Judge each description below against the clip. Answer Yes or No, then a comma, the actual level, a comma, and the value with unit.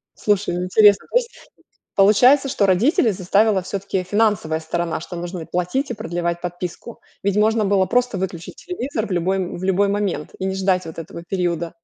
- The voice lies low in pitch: No, high, 190 Hz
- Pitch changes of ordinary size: Yes, average, 3.2 semitones